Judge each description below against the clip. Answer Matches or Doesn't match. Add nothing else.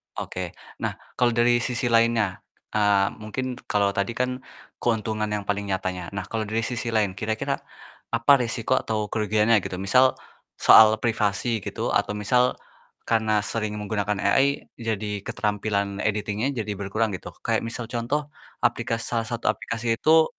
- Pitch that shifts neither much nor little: Doesn't match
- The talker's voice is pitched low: Matches